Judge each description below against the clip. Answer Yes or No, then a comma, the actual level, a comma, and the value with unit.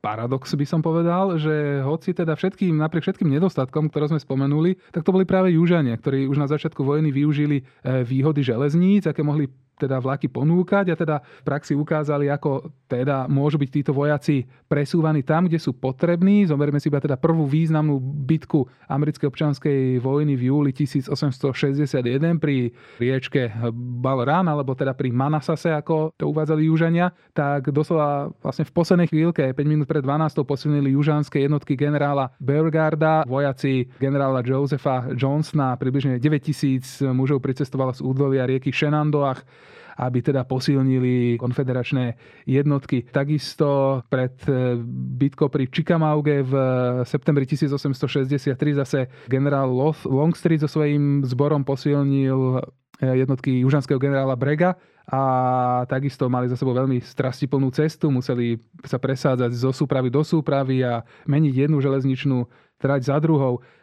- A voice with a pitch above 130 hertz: Yes, medium, 140 Hz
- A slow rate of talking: No, average, 135 wpm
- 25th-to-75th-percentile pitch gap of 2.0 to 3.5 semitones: Yes, narrow, 2.6 semitones